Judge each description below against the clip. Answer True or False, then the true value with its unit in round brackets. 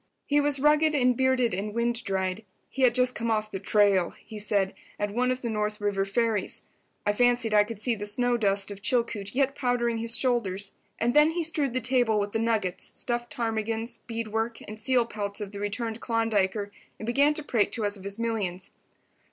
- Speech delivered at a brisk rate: True (210 wpm)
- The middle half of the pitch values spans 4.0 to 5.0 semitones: False (3.1 semitones)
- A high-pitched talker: True (225 Hz)